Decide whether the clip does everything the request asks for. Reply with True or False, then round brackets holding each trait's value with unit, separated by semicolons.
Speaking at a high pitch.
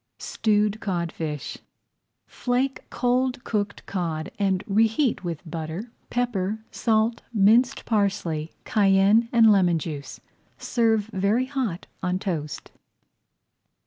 True (205 Hz)